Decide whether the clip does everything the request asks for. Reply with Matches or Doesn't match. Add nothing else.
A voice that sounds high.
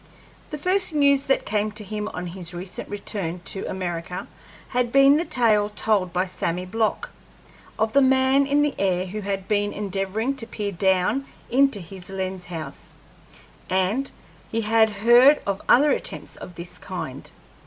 Matches